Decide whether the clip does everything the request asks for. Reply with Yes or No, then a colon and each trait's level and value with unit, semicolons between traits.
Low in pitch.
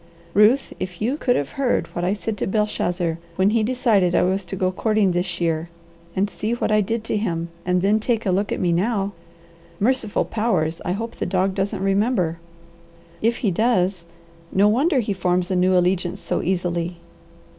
No: high, 195 Hz